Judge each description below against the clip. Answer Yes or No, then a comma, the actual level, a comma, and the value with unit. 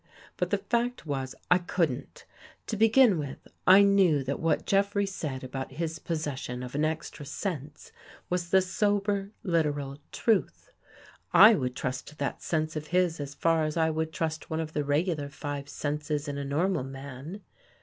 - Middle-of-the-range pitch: Yes, medium, 155 Hz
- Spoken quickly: No, average, 170 wpm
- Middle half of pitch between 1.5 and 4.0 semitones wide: No, average, 4.4 semitones